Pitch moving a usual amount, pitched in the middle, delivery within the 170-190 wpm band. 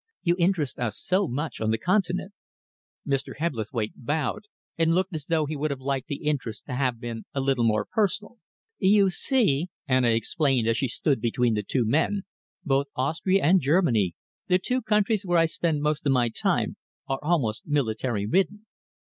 No: wide, 6.5 semitones; medium, 145 Hz; average, 180 wpm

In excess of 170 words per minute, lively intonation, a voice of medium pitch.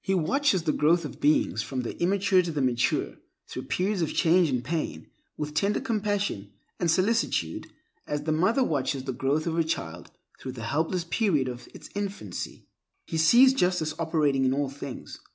Yes: average, 180 wpm; wide, 5.7 semitones; medium, 160 Hz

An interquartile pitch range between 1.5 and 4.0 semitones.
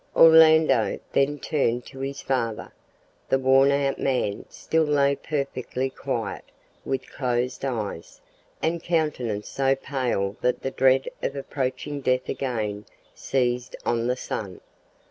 Yes: narrow, 2.4 semitones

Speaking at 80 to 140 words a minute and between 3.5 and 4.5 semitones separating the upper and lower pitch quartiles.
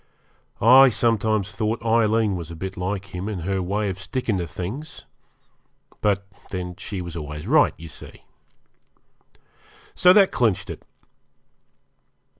Yes: slow, 135 wpm; average, 3.9 semitones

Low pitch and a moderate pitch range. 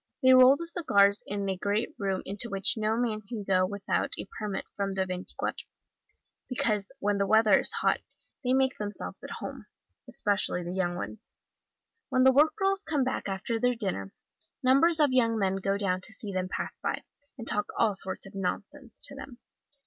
No: high, 210 Hz; average, 4.6 semitones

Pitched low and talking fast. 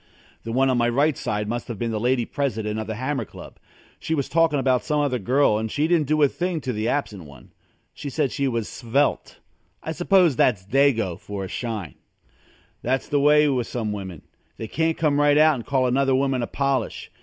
Yes: low, 130 Hz; fast, 210 wpm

